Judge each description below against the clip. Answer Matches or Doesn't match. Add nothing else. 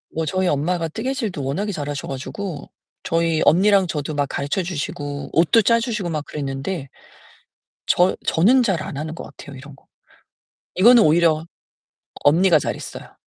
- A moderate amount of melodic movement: Matches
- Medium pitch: Matches